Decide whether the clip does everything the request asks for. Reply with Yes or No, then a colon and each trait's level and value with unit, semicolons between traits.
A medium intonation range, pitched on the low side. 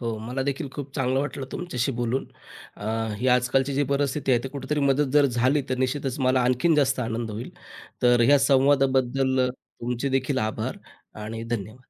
No: narrow, 2.2 semitones; low, 130 Hz